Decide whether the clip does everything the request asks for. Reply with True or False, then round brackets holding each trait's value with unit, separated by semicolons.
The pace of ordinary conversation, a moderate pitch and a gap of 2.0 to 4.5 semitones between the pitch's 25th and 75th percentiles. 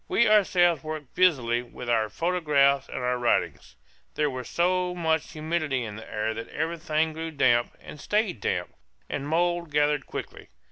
False (160 wpm; 155 Hz; 5.4 semitones)